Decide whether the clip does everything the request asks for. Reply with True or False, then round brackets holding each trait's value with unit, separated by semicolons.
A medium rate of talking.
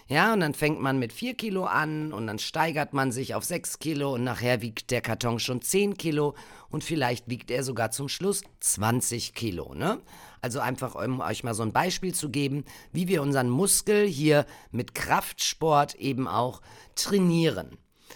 True (180 wpm)